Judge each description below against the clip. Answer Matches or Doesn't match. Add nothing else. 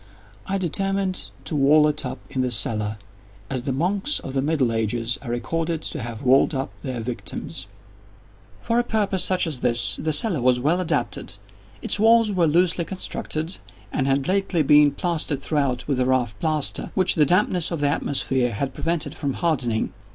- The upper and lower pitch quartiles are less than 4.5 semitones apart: Doesn't match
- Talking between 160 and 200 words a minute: Matches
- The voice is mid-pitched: Matches